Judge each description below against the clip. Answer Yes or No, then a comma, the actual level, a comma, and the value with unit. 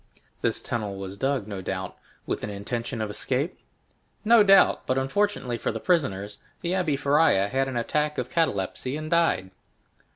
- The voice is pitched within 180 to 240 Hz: No, low, 130 Hz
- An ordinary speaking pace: Yes, average, 165 wpm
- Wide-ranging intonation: Yes, wide, 7.2 semitones